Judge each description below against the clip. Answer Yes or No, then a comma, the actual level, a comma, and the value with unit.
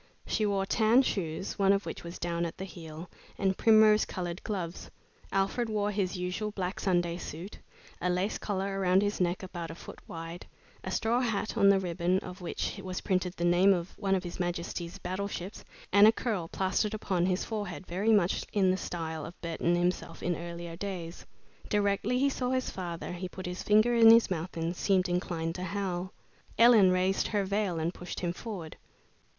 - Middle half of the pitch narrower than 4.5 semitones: Yes, average, 2.7 semitones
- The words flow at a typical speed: Yes, average, 190 wpm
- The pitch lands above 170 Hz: Yes, medium, 185 Hz